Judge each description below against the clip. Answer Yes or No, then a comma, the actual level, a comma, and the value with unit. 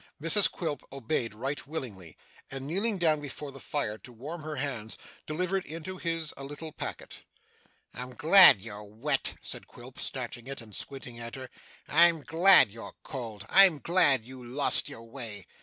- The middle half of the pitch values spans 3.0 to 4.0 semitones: No, wide, 5.6 semitones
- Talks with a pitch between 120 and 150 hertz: Yes, medium, 140 Hz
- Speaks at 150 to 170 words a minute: Yes, average, 165 wpm